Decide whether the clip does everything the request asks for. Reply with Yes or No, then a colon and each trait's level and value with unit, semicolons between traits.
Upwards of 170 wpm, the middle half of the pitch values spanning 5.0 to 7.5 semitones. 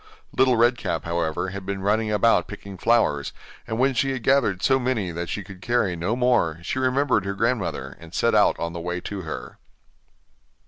Yes: average, 195 wpm; wide, 5.6 semitones